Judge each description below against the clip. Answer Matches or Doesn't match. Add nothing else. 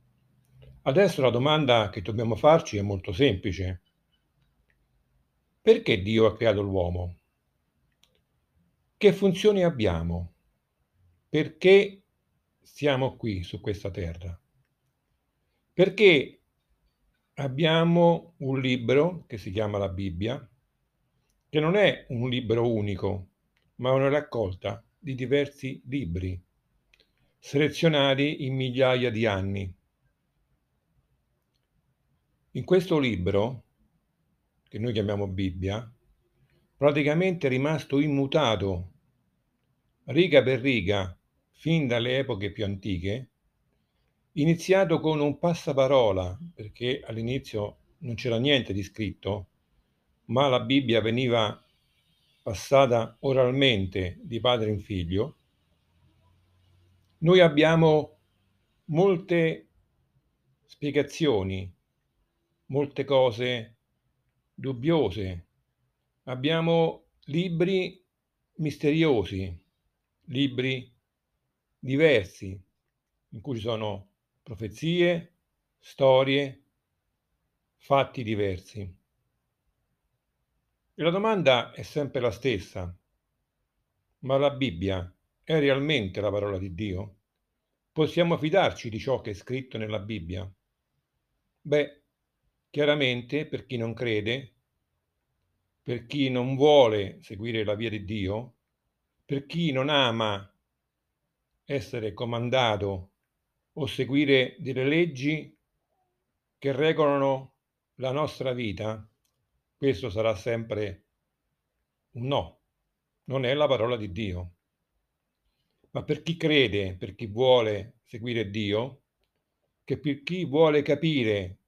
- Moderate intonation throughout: Doesn't match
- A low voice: Matches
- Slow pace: Matches